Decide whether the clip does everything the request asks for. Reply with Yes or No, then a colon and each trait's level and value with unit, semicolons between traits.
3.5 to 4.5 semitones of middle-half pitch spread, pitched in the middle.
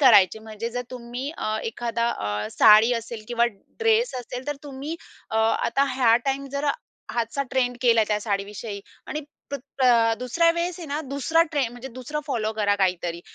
No: average, 4.2 semitones; high, 240 Hz